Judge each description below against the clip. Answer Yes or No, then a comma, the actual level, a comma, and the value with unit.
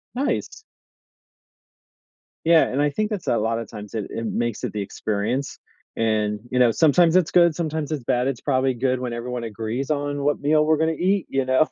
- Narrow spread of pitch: No, average, 5.2 semitones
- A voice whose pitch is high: No, low, 135 Hz